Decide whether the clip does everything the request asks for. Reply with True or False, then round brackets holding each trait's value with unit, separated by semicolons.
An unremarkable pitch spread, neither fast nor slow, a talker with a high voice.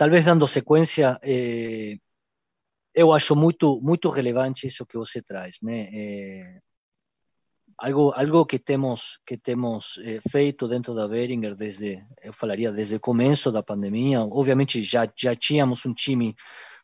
False (4.1 semitones; 135 wpm; 125 Hz)